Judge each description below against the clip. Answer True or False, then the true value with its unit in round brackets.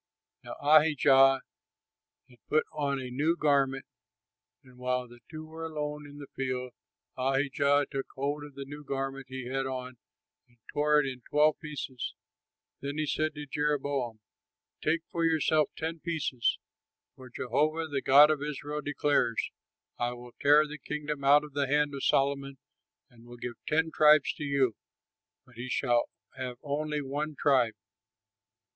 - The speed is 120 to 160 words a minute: True (155 wpm)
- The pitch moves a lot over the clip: False (2.4 semitones)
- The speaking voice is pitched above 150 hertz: False (140 Hz)